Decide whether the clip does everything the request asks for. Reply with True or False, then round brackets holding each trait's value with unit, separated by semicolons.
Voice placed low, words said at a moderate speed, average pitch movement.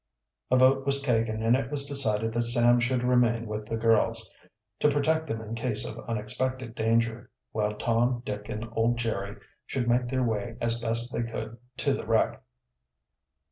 False (115 Hz; 180 wpm; 2.1 semitones)